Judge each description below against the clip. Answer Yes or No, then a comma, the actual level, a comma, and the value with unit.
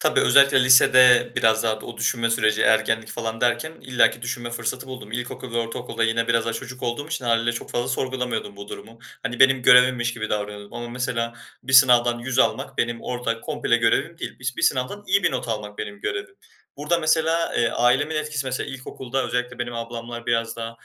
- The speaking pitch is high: No, low, 120 Hz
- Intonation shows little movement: Yes, narrow, 2.1 semitones